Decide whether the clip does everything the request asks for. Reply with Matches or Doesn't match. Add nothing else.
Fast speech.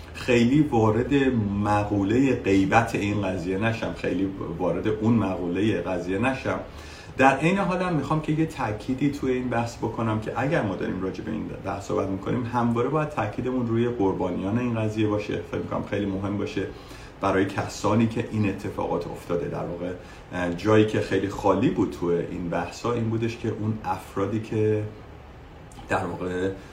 Matches